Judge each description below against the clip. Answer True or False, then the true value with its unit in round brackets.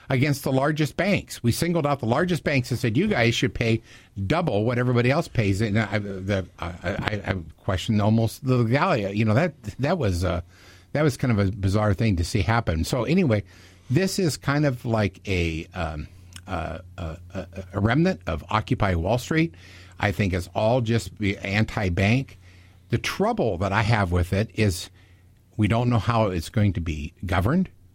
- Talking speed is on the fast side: False (185 wpm)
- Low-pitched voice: True (105 Hz)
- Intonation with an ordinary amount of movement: True (4.7 semitones)